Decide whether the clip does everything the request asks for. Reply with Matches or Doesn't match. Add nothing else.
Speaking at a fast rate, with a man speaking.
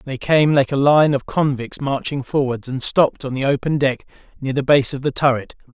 Matches